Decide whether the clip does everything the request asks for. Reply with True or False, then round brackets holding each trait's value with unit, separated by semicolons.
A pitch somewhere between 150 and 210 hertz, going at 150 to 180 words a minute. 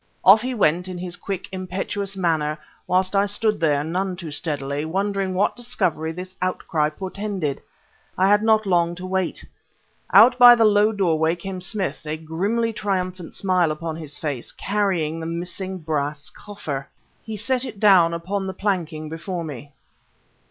True (185 Hz; 160 wpm)